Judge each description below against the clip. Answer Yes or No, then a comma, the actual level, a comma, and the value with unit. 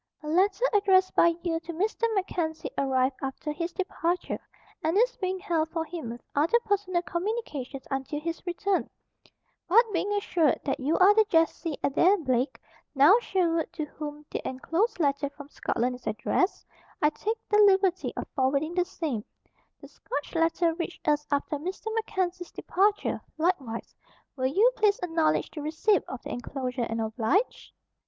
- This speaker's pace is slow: No, average, 160 wpm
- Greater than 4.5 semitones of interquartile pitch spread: Yes, average, 4.9 semitones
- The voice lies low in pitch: No, very high, 330 Hz